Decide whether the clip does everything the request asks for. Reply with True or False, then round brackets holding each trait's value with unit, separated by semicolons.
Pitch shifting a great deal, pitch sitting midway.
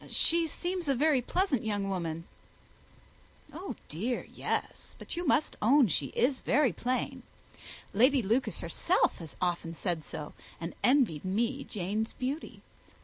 False (7.6 semitones; 240 Hz)